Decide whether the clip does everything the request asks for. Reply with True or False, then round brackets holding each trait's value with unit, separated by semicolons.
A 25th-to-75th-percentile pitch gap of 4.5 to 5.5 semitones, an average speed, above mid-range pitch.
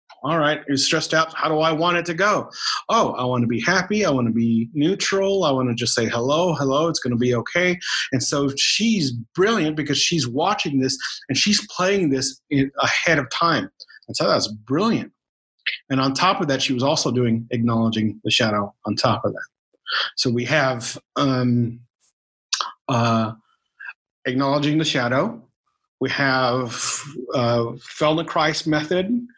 False (5.1 semitones; 170 wpm; 135 Hz)